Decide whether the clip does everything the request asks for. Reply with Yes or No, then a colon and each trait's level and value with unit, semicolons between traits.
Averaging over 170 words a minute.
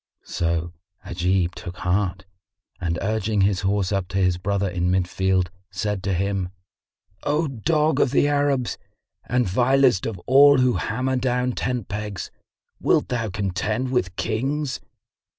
No: average, 145 wpm